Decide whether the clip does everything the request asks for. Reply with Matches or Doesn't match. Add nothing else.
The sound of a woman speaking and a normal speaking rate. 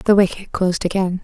Matches